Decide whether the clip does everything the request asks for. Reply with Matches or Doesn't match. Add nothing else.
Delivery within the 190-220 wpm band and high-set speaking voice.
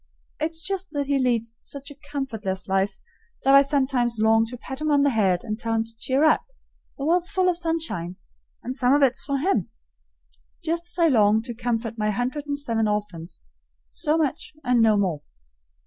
Matches